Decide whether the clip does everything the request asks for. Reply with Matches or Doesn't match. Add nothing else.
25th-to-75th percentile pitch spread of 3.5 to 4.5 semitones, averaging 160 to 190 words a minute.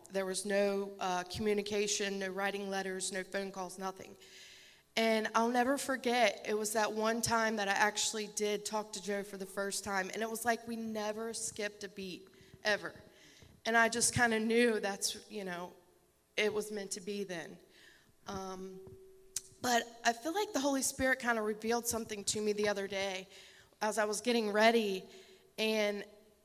Doesn't match